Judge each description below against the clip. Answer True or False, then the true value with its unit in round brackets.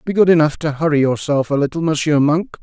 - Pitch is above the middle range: False (150 Hz)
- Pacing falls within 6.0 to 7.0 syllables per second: True (6.1 syllables/s)